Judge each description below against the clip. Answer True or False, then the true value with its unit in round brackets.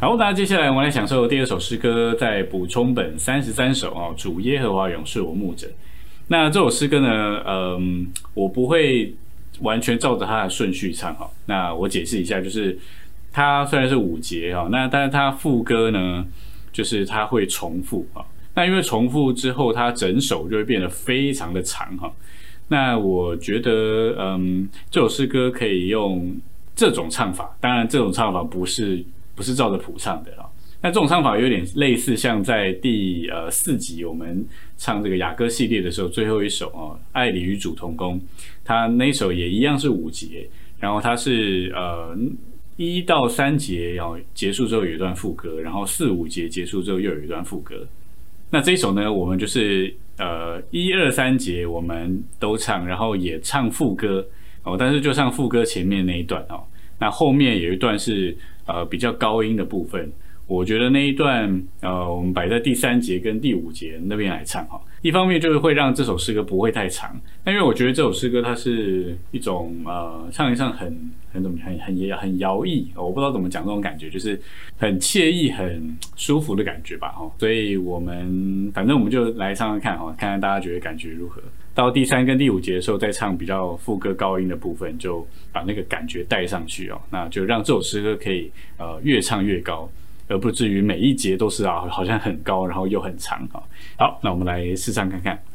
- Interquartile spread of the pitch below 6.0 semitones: True (5.1 semitones)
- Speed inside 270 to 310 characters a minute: True (290 characters per minute)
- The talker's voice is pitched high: False (100 Hz)